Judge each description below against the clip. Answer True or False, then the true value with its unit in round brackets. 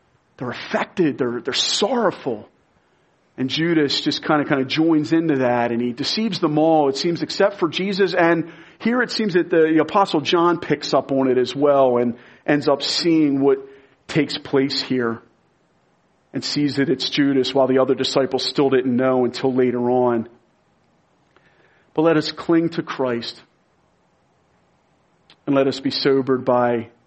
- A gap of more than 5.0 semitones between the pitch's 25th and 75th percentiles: False (4.0 semitones)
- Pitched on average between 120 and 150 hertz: True (140 Hz)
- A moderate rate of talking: True (165 wpm)